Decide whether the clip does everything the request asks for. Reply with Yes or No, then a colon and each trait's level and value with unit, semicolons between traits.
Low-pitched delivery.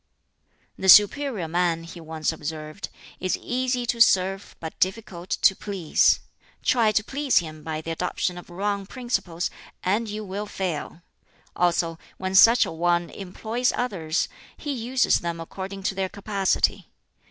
No: high, 190 Hz